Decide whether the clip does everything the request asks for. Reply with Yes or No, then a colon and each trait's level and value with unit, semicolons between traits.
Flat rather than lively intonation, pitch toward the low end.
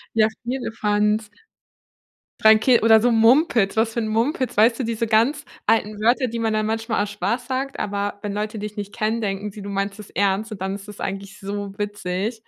No: narrow, 2.1 semitones; high, 215 Hz